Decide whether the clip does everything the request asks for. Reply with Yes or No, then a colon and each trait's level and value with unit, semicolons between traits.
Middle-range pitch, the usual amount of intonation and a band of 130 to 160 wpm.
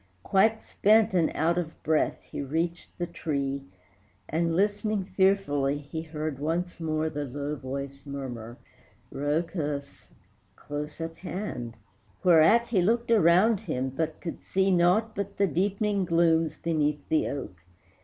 Yes: medium, 165 Hz; average, 4.7 semitones; slow, 135 wpm